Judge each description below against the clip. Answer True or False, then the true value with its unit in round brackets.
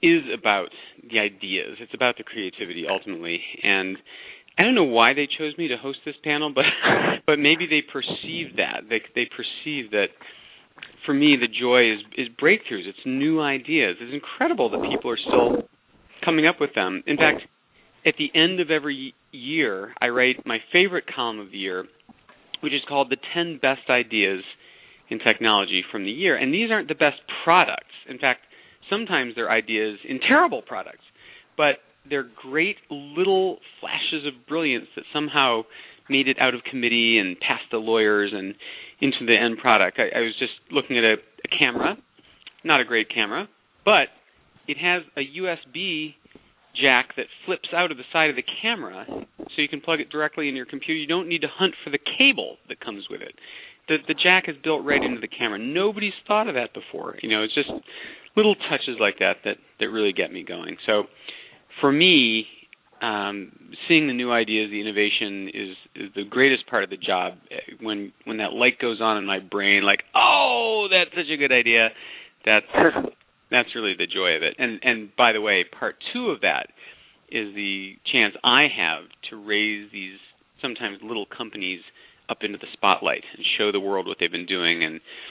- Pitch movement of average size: False (6.7 semitones)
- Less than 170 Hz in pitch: True (140 Hz)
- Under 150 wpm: False (190 wpm)